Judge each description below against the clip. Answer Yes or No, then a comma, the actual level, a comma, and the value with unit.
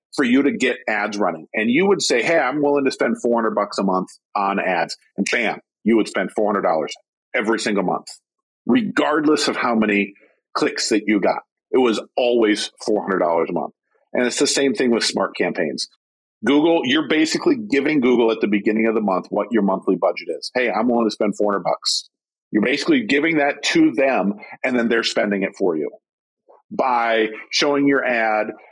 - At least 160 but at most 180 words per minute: No, average, 190 wpm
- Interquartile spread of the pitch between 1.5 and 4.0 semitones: No, average, 4.9 semitones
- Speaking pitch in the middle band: No, low, 120 Hz